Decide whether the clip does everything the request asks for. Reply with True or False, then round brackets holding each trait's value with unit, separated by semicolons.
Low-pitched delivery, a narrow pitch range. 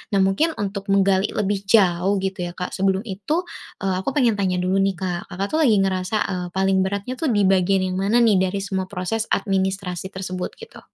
False (195 Hz; 1.5 semitones)